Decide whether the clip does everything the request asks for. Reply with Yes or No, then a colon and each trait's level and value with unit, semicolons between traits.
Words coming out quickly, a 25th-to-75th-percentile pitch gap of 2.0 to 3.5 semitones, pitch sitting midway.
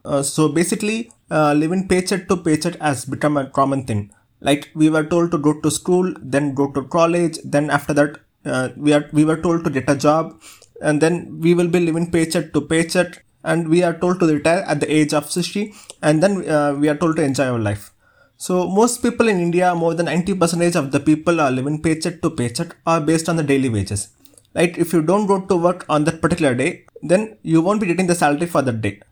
Yes: fast, 230 wpm; average, 3.1 semitones; medium, 160 Hz